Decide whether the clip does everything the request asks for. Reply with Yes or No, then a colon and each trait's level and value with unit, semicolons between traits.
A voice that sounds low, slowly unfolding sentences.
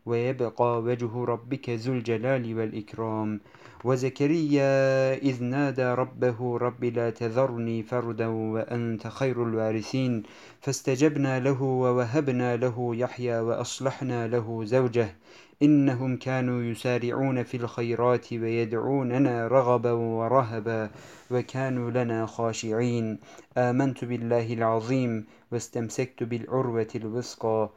Yes: low, 120 Hz; slow, 90 wpm